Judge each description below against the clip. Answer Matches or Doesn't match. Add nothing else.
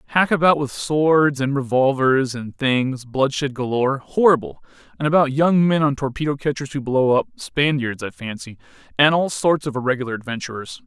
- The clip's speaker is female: Doesn't match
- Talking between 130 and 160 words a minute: Matches